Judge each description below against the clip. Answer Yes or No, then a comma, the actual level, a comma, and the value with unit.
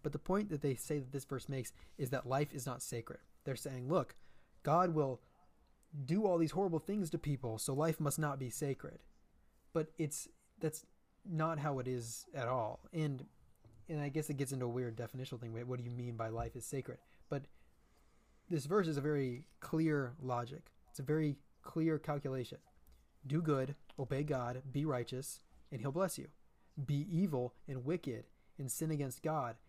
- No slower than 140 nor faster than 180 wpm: No, average, 190 wpm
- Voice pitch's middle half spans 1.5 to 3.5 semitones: No, average, 3.9 semitones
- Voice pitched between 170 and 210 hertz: No, medium, 140 Hz